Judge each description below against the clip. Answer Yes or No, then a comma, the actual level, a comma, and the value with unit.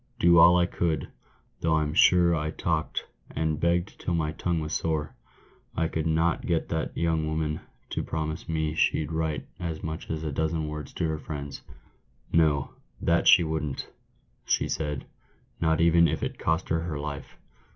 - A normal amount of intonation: No, narrow, 1.4 semitones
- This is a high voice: No, very low, 80 Hz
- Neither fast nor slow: Yes, average, 180 wpm